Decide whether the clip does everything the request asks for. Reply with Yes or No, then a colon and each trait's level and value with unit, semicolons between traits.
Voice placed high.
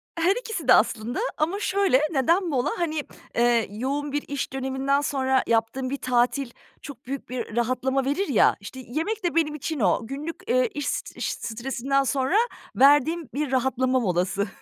Yes: very high, 270 Hz